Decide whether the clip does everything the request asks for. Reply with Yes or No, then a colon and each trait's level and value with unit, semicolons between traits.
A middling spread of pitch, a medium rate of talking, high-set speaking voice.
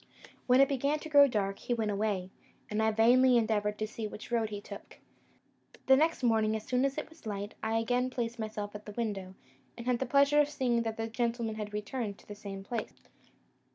No: average, 3.2 semitones; fast, 220 wpm; high, 225 Hz